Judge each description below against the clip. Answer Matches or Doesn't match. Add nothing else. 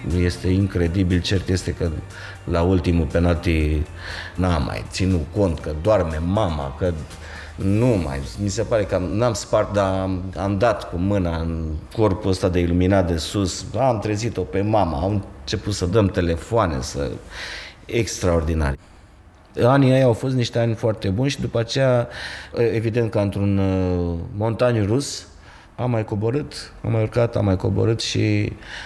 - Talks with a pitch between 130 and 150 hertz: Doesn't match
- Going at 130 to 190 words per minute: Matches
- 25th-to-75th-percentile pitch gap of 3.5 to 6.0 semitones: Matches